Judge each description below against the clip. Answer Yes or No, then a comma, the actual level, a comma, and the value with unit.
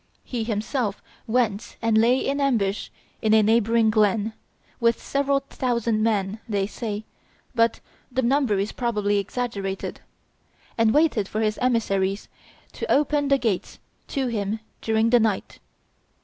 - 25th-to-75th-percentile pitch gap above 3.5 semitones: No, average, 2.8 semitones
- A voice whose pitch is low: No, high, 225 Hz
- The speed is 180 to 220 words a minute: No, slow, 135 wpm